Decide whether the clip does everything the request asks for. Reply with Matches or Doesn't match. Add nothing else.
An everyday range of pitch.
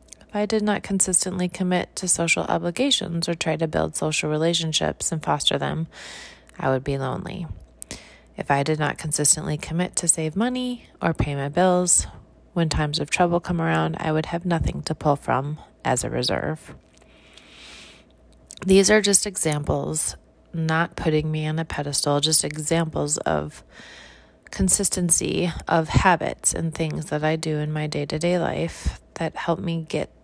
Matches